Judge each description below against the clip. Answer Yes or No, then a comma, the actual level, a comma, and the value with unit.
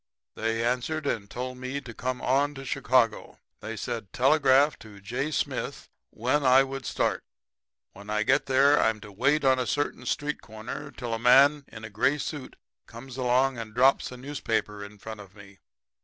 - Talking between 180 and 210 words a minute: Yes, average, 185 wpm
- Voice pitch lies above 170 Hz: No, low, 125 Hz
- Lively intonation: No, average, 3.5 semitones